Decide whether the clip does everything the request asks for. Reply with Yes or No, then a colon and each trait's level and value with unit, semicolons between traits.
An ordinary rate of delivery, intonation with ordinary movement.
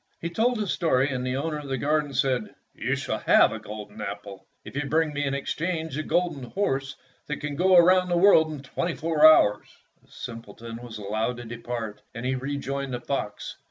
No: fast, 210 wpm; average, 4.9 semitones